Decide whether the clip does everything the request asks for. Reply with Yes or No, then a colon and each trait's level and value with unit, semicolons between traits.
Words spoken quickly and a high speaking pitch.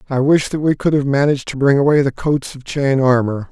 No: fast, 255 wpm; medium, 140 Hz